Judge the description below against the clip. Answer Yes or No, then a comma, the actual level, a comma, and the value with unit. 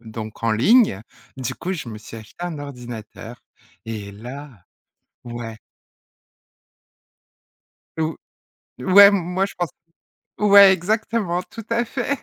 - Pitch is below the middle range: No, medium, 145 Hz